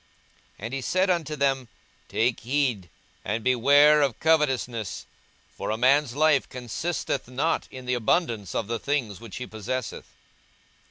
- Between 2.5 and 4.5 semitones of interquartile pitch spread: Yes, average, 4.0 semitones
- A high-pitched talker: No, low, 130 Hz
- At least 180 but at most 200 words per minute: No, average, 150 wpm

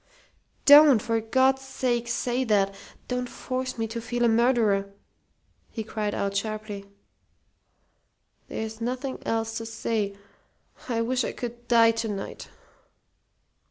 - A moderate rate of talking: No, slow, 125 wpm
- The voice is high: Yes, high, 230 Hz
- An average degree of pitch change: No, narrow, 2.3 semitones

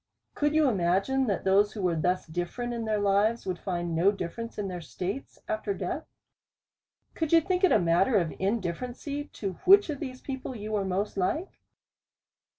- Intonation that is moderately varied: No, wide, 5.8 semitones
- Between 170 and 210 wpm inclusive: Yes, average, 180 wpm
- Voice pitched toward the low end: No, high, 205 Hz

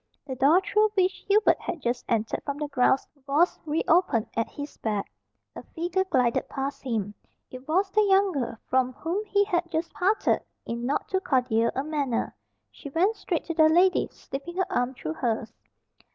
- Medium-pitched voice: No, very high, 295 Hz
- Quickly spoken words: No, average, 185 wpm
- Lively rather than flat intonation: Yes, wide, 6.5 semitones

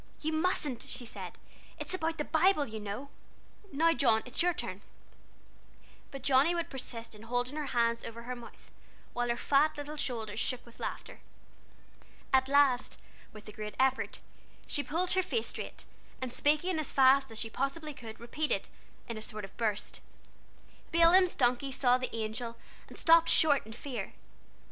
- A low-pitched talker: No, very high, 260 Hz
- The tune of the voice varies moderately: Yes, average, 4.7 semitones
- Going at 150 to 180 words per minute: Yes, average, 170 wpm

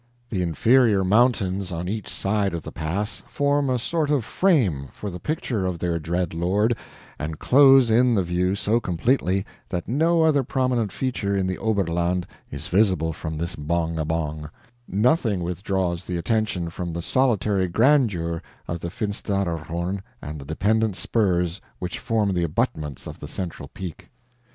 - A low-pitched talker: Yes, very low, 95 Hz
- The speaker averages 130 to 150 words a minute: No, average, 160 wpm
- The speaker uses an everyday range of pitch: Yes, average, 4.8 semitones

